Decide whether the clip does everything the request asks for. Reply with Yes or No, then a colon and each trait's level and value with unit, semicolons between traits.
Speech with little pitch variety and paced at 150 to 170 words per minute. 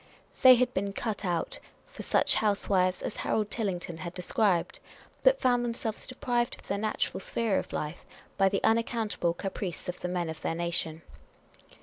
No: average, 4.6 semitones; average, 165 wpm